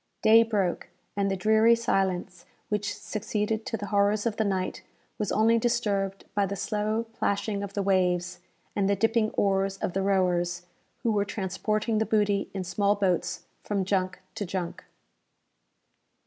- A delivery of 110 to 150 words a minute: No, average, 160 wpm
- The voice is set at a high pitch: Yes, high, 200 Hz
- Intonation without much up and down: Yes, narrow, 2.1 semitones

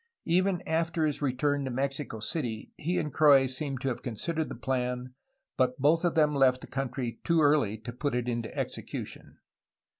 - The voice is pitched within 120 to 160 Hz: Yes, low, 135 Hz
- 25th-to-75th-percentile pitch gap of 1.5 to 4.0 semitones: Yes, average, 3.6 semitones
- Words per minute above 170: Yes, average, 180 wpm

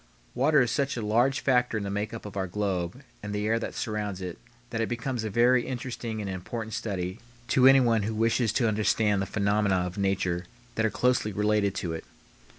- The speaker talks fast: Yes, fast, 210 wpm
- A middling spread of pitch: Yes, average, 3.2 semitones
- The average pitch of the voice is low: Yes, low, 110 Hz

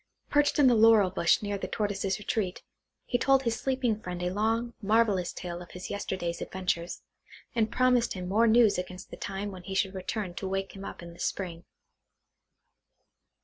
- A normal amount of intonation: Yes, average, 3.8 semitones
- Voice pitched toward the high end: Yes, high, 200 Hz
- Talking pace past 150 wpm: Yes, average, 185 wpm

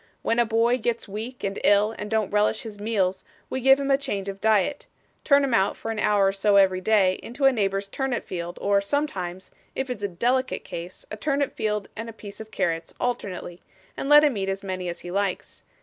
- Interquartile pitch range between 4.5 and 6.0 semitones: No, average, 3.8 semitones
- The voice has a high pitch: Yes, high, 210 Hz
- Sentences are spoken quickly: Yes, fast, 225 wpm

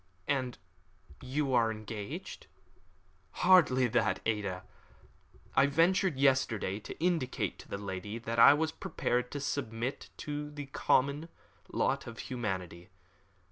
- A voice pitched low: Yes, low, 125 Hz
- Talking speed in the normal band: No, slow, 120 wpm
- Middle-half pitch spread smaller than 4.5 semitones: No, average, 4.8 semitones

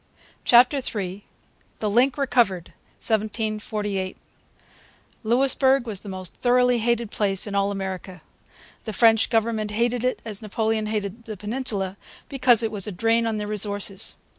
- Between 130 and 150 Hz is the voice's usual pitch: No, high, 215 Hz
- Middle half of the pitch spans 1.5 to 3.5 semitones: Yes, average, 2.8 semitones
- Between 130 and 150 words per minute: Yes, average, 140 wpm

